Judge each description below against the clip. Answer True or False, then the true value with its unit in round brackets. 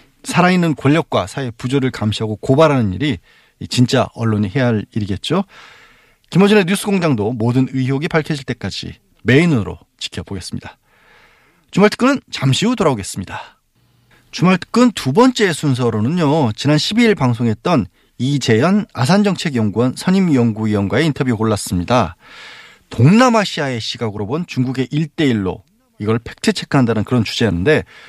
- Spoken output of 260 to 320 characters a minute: False (340 characters per minute)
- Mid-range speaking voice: False (130 Hz)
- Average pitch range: False (7.2 semitones)